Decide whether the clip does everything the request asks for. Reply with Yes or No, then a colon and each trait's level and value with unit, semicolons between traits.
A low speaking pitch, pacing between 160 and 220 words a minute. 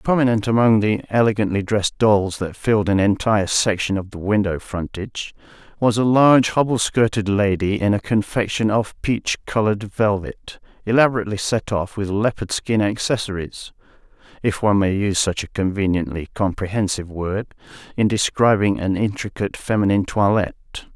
No: low, 105 Hz; average, 145 wpm